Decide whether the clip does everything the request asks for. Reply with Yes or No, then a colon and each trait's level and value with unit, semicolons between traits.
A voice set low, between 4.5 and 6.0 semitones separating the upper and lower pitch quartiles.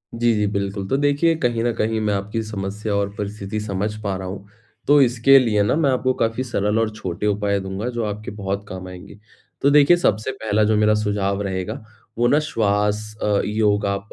No: low, 105 Hz; narrow, 2.5 semitones